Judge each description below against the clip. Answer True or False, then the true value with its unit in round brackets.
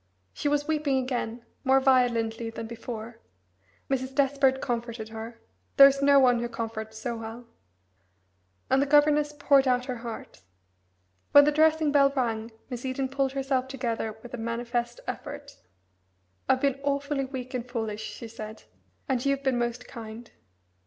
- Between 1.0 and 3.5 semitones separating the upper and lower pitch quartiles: True (3.0 semitones)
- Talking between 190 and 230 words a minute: False (155 wpm)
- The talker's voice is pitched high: True (255 Hz)